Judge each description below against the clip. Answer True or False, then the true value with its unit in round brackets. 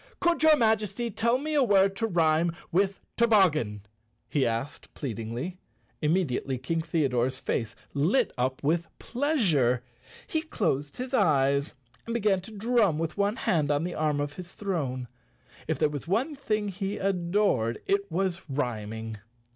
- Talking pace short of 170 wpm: True (155 wpm)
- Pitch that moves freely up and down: True (7.0 semitones)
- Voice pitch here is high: False (170 Hz)